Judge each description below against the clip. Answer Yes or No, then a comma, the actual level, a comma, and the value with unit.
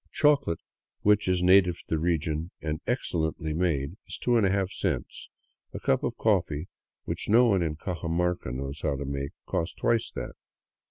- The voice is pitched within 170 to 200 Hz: No, very low, 85 Hz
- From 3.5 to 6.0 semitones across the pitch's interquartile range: Yes, average, 4.1 semitones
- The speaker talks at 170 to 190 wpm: No, average, 160 wpm